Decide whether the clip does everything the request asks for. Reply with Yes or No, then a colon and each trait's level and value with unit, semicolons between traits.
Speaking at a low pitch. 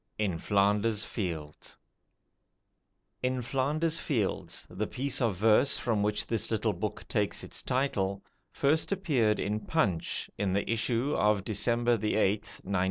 Yes: low, 110 Hz